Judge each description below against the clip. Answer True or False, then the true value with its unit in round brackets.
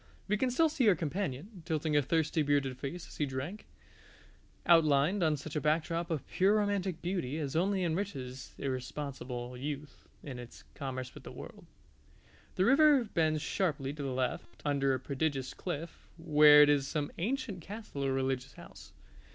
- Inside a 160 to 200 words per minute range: True (165 wpm)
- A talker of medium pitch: True (150 Hz)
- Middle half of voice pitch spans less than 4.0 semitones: False (4.9 semitones)